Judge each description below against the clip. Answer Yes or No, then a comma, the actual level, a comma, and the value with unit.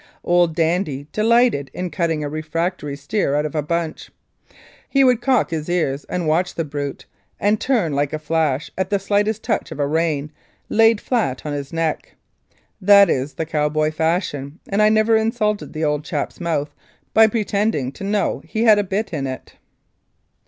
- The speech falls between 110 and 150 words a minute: No, average, 180 wpm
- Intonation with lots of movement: Yes, wide, 5.7 semitones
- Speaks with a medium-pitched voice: Yes, medium, 165 Hz